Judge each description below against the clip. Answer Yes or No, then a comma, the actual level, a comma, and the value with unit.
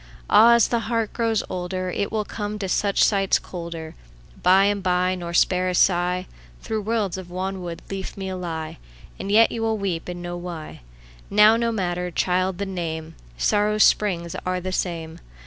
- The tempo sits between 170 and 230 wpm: No, average, 150 wpm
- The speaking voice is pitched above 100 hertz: Yes, medium, 185 Hz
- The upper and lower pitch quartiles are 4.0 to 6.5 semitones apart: No, average, 3.0 semitones